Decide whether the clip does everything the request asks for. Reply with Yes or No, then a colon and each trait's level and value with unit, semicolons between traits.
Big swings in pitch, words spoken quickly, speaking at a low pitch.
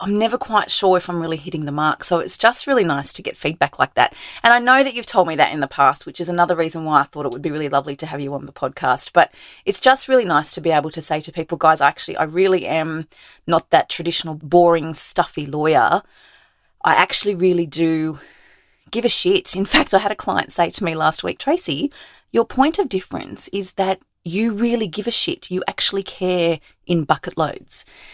No: wide, 6.2 semitones; fast, 230 wpm; medium, 175 Hz